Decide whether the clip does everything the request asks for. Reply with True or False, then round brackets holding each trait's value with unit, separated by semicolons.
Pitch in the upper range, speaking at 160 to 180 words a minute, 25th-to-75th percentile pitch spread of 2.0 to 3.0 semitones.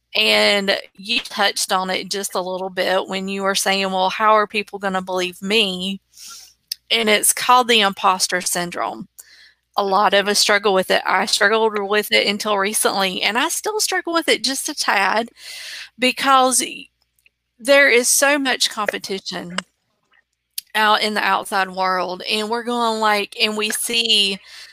False (210 Hz; 165 wpm; 3.8 semitones)